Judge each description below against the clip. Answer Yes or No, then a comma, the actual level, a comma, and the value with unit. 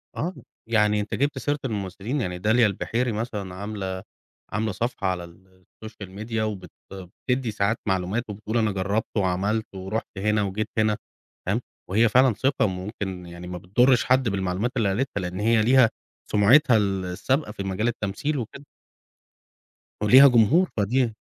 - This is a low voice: Yes, low, 105 Hz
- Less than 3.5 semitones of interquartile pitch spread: No, average, 3.8 semitones